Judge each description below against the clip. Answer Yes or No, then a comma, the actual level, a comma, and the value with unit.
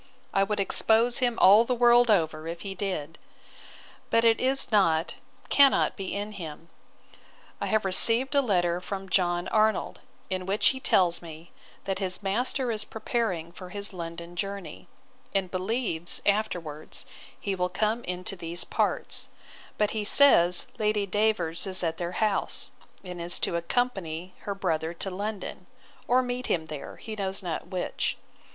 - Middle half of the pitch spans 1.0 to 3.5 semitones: No, average, 3.9 semitones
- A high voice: Yes, high, 195 Hz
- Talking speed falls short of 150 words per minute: No, average, 160 wpm